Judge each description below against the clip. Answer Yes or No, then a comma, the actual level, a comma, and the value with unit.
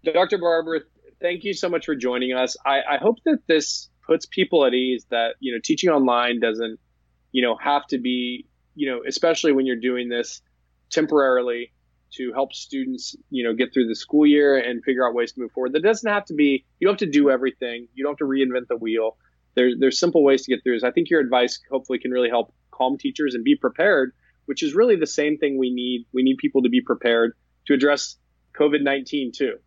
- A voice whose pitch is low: Yes, low, 130 Hz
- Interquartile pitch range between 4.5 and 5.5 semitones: No, average, 3.8 semitones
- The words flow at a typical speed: No, fast, 225 wpm